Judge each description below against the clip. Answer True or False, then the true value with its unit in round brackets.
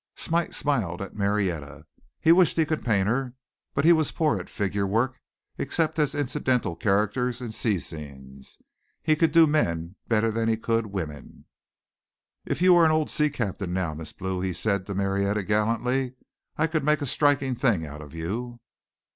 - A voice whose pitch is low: True (115 Hz)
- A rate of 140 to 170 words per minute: False (180 wpm)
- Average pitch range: False (7.2 semitones)